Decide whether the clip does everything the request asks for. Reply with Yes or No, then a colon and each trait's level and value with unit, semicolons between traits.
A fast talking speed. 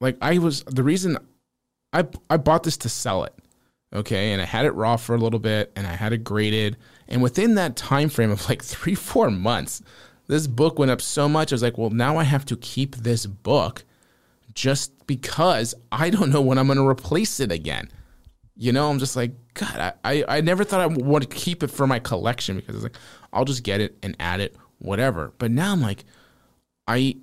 Yes: fast, 225 wpm